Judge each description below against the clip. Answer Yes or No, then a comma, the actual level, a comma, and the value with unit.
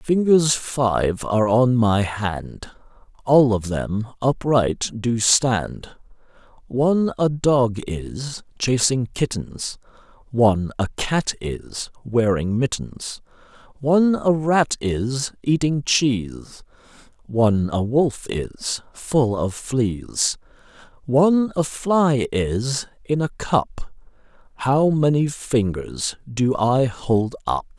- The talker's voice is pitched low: Yes, low, 125 Hz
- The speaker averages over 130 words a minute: No, slow, 110 wpm